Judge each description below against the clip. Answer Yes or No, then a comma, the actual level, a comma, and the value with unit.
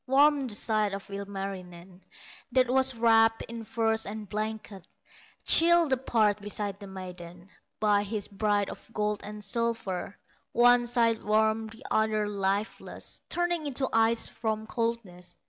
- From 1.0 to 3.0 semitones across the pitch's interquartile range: Yes, narrow, 2.6 semitones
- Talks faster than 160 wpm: No, average, 140 wpm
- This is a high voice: Yes, high, 220 Hz